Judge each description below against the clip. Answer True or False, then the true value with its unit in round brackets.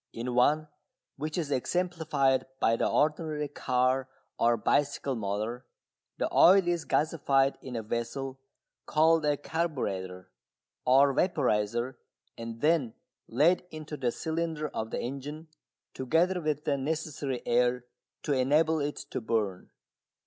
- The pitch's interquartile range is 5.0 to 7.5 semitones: False (4.3 semitones)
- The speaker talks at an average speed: False (125 wpm)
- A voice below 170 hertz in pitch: True (140 Hz)